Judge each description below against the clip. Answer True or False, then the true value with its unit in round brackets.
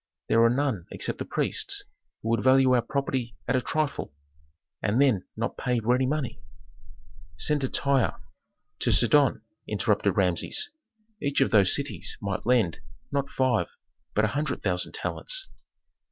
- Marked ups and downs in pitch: False (4.1 semitones)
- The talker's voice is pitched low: True (125 Hz)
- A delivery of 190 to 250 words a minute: False (150 wpm)